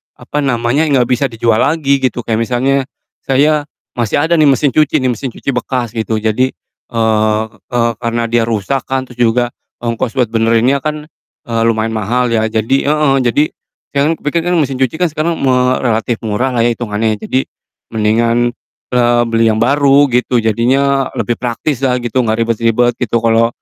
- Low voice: Yes, low, 120 Hz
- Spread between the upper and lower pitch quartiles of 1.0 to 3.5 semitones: Yes, average, 3.0 semitones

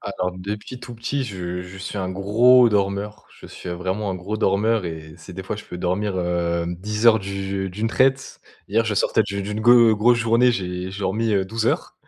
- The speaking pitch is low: Yes, low, 100 Hz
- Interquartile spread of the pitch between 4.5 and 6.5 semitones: No, average, 3.3 semitones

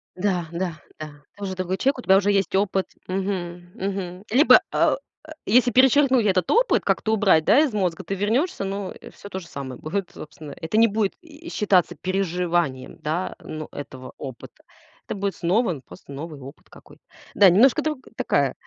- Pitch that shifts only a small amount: No, average, 3.7 semitones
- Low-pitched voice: No, high, 190 Hz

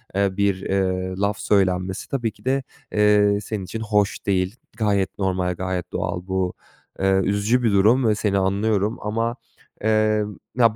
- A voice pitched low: Yes, low, 100 Hz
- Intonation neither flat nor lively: No, narrow, 2.3 semitones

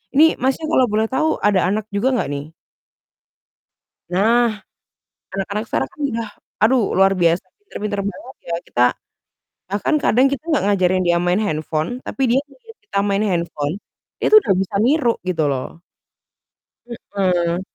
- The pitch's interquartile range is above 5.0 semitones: Yes, wide, 5.5 semitones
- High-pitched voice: Yes, high, 200 Hz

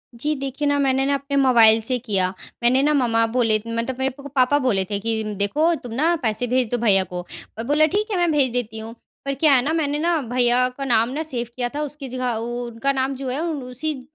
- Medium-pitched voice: No, very high, 255 Hz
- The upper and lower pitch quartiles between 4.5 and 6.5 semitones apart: No, average, 3.7 semitones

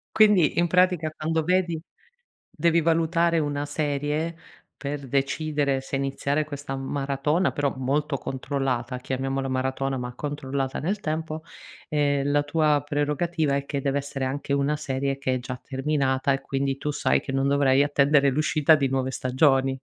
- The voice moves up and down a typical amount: No, narrow, 2.3 semitones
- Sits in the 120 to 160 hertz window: Yes, medium, 140 Hz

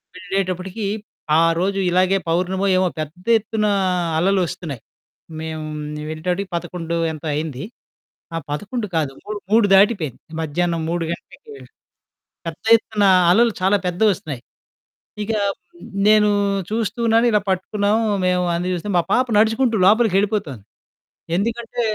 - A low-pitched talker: No, high, 190 Hz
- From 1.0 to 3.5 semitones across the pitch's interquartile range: No, average, 4.0 semitones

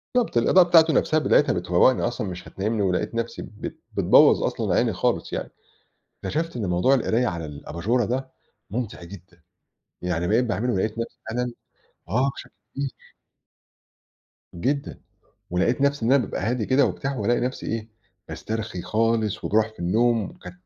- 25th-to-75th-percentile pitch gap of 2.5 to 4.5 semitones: No, average, 4.9 semitones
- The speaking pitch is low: Yes, low, 115 Hz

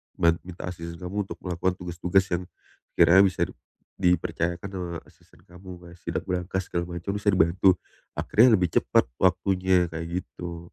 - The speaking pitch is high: No, very low, 90 Hz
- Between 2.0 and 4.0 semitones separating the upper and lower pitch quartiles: No, narrow, 1.5 semitones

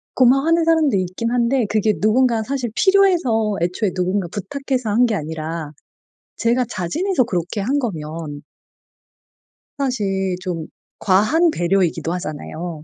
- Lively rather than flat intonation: Yes, wide, 6.5 semitones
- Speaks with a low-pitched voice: No, high, 215 Hz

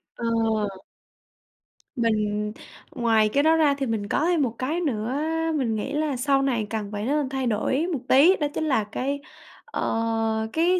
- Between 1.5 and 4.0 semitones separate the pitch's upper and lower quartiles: No, average, 4.8 semitones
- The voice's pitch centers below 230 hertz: No, very high, 255 Hz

